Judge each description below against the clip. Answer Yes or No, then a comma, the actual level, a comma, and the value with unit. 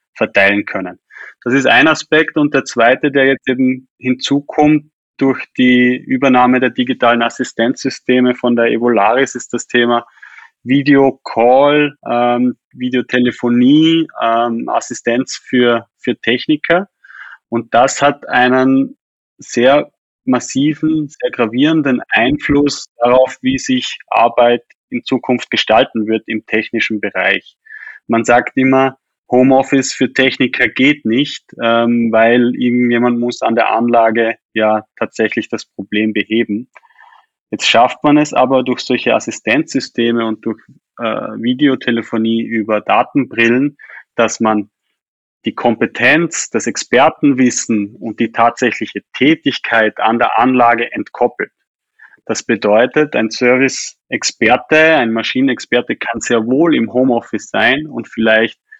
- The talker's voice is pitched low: Yes, low, 125 Hz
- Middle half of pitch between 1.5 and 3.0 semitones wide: Yes, average, 2.7 semitones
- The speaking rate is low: Yes, slow, 115 wpm